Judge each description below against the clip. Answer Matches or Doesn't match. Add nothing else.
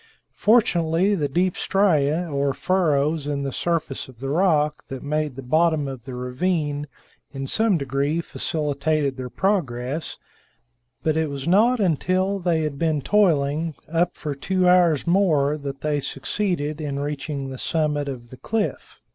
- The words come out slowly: Doesn't match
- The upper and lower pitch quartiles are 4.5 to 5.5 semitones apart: Doesn't match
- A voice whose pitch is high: Doesn't match